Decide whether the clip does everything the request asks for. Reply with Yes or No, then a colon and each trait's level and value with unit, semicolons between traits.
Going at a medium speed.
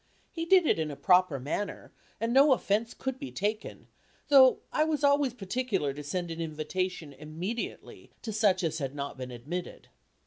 Yes: average, 175 wpm